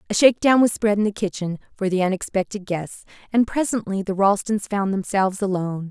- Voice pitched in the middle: No, high, 200 Hz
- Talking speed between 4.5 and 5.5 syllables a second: No, 5.8 syllables/s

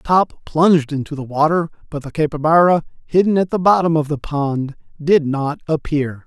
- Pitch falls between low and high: Yes, medium, 155 Hz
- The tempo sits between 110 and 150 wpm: No, average, 170 wpm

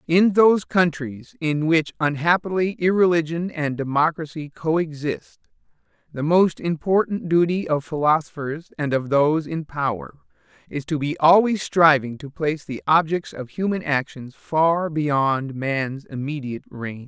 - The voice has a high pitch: No, medium, 155 Hz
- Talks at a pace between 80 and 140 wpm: Yes, slow, 135 wpm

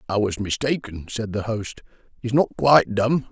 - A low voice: Yes, low, 115 Hz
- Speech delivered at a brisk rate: No, average, 180 wpm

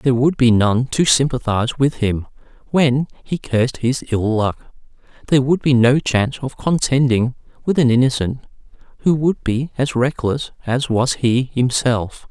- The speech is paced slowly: No, average, 160 wpm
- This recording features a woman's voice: No, male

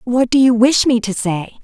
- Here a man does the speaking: No, female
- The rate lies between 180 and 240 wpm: No, fast, 255 wpm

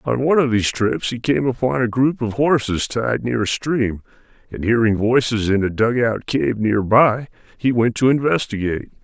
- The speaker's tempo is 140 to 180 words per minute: No, average, 195 wpm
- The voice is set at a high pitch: No, low, 120 Hz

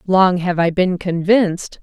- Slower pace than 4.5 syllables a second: Yes, 4.1 syllables/s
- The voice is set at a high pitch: No, medium, 180 Hz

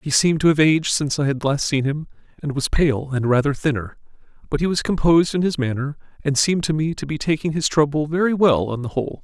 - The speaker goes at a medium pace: No, fast, 245 wpm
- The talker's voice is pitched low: No, medium, 145 Hz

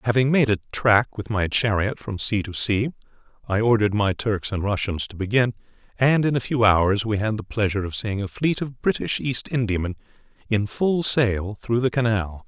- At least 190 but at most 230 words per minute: Yes, average, 200 wpm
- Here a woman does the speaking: No, male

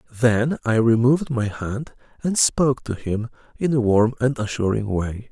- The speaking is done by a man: Yes, male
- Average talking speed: Yes, average, 170 wpm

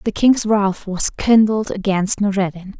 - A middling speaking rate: Yes, average, 150 wpm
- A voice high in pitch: Yes, high, 200 Hz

